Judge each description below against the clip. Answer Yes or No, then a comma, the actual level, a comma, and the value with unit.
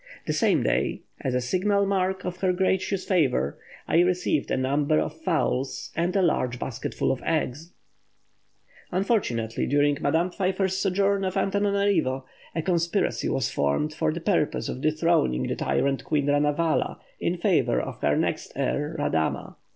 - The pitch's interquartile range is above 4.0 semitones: Yes, average, 5.2 semitones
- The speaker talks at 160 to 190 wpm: No, average, 150 wpm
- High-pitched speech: No, medium, 165 Hz